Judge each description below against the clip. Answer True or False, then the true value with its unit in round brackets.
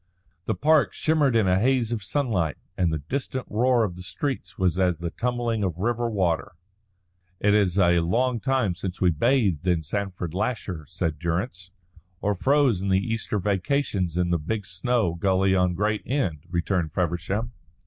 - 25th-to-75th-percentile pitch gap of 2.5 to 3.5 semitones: False (5.2 semitones)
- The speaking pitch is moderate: False (95 Hz)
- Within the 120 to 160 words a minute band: False (170 wpm)